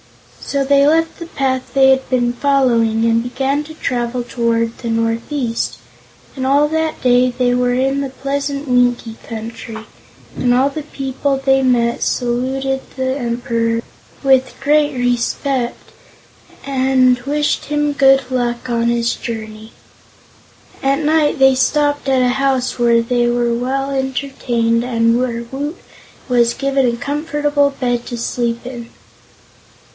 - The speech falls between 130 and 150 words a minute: Yes, average, 140 wpm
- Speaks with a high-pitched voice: Yes, very high, 255 Hz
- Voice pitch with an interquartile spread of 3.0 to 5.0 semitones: No, narrow, 2.6 semitones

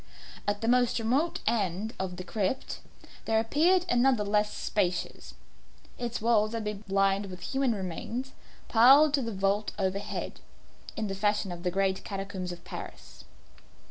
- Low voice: No, high, 210 Hz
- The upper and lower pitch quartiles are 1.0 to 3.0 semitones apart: No, average, 3.5 semitones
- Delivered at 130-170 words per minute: Yes, average, 150 wpm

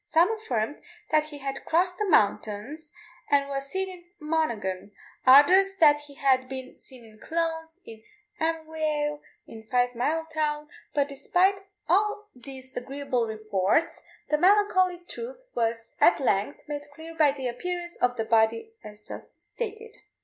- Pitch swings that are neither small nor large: No, wide, 5.7 semitones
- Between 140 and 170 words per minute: Yes, average, 150 wpm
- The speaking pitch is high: Yes, very high, 295 Hz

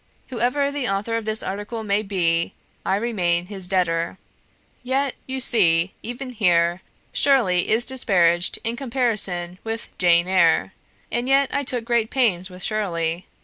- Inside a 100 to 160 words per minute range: Yes, average, 145 wpm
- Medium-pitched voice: No, high, 205 Hz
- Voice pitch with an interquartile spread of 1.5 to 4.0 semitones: No, average, 5.3 semitones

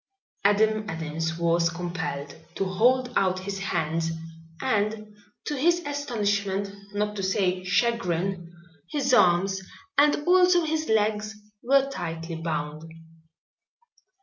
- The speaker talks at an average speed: No, slow, 110 wpm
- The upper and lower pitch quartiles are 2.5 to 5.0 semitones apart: No, wide, 5.5 semitones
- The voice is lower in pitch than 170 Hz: No, high, 200 Hz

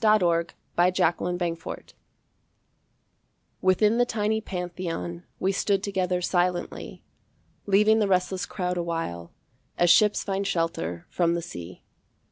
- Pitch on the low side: No, medium, 180 Hz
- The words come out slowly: Yes, slow, 115 wpm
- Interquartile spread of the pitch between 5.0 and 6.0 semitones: No, narrow, 2.5 semitones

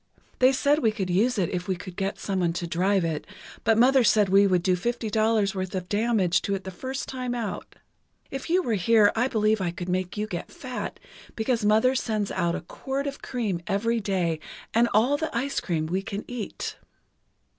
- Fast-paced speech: Yes, fast, 210 wpm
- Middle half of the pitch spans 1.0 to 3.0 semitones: No, average, 4.4 semitones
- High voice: Yes, high, 210 Hz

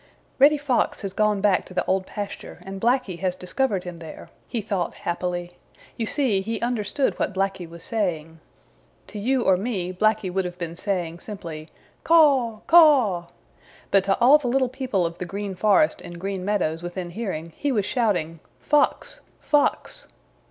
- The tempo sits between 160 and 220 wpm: Yes, average, 170 wpm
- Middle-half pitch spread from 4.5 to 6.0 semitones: Yes, average, 5.3 semitones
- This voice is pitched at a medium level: No, high, 195 Hz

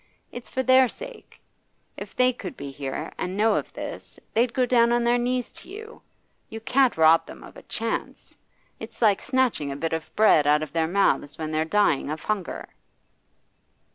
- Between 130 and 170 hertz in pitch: No, high, 215 Hz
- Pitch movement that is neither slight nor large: No, wide, 7.8 semitones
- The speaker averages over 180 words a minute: Yes, average, 190 wpm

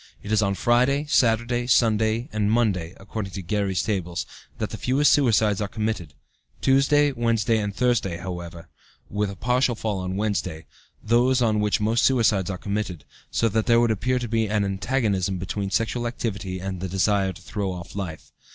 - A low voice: Yes, low, 105 Hz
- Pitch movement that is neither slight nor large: Yes, average, 3.6 semitones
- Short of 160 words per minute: No, average, 180 wpm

